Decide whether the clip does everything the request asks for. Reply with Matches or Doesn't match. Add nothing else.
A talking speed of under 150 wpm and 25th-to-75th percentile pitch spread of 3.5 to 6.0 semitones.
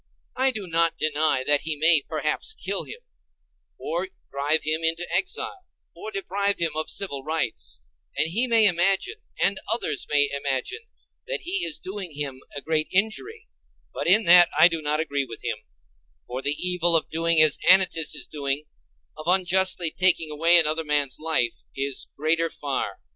Doesn't match